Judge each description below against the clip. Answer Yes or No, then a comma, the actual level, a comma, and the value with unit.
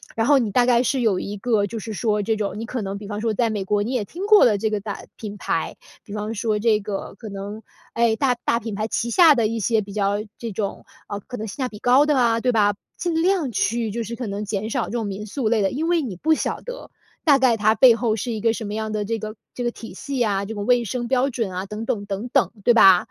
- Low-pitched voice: No, high, 225 Hz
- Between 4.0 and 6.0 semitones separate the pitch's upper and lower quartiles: No, average, 2.9 semitones